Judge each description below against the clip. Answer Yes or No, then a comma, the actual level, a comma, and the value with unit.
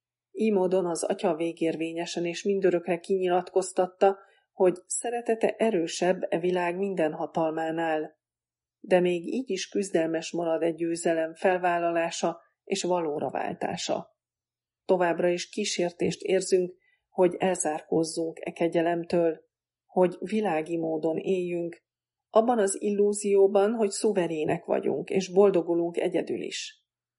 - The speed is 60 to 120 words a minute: Yes, slow, 105 wpm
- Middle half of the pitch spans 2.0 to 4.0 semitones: Yes, average, 2.8 semitones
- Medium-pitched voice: Yes, medium, 180 Hz